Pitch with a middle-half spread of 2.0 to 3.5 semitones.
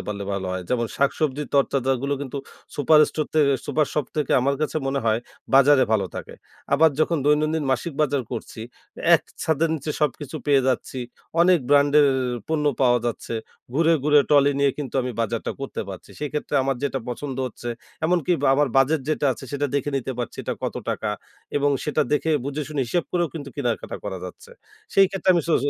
Yes: average, 2.7 semitones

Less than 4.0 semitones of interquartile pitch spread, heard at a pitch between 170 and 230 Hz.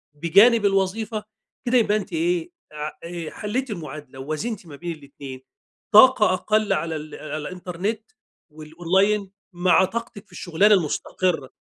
No: wide, 5.5 semitones; medium, 185 Hz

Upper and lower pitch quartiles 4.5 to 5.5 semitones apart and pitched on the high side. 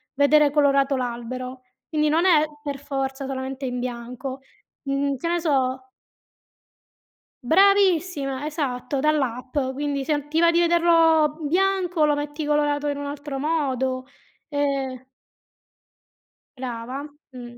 No: average, 2.7 semitones; very high, 285 Hz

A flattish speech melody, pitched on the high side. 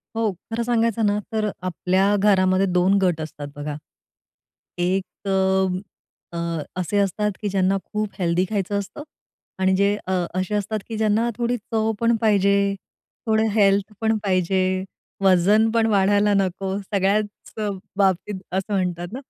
Yes: narrow, 2.3 semitones; high, 200 Hz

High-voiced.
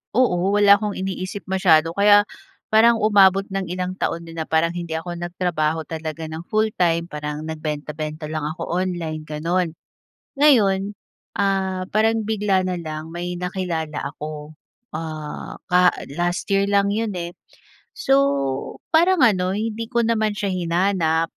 No: medium, 180 Hz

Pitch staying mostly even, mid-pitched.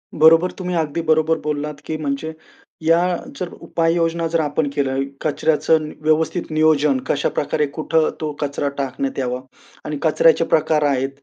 Yes: narrow, 2.0 semitones; medium, 155 Hz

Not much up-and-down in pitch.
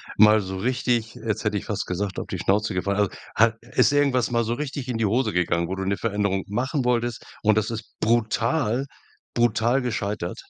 No: average, 3.0 semitones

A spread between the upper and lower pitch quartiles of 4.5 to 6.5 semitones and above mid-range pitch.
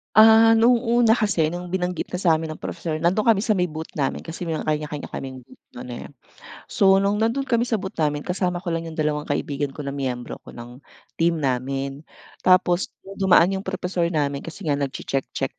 No: average, 5.1 semitones; medium, 170 Hz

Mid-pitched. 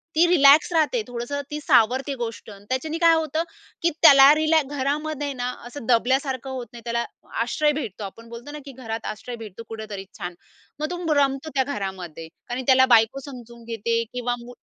No: very high, 260 Hz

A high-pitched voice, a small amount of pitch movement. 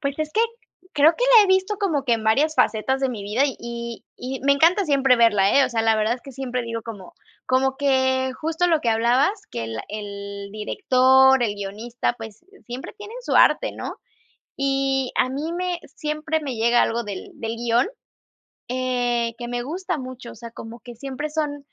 No: very high, 255 Hz; average, 3.9 semitones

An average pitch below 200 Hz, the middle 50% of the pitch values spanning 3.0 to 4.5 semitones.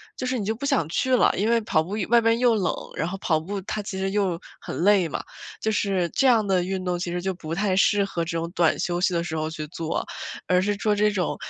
Yes: high, 190 Hz; average, 3.4 semitones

